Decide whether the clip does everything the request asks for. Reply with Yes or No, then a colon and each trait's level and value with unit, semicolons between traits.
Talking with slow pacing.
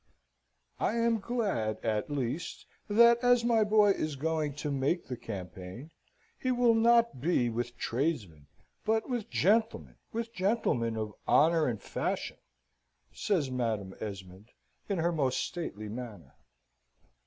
Yes: slow, 130 wpm